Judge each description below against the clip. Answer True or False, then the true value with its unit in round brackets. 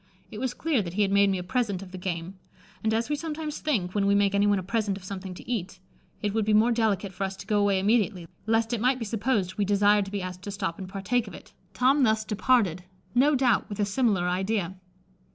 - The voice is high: True (205 Hz)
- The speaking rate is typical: False (250 wpm)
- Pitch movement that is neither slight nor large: True (3.1 semitones)